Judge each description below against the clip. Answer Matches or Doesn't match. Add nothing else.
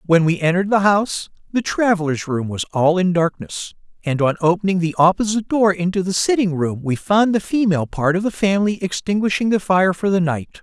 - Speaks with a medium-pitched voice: Matches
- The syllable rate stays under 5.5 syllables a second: Doesn't match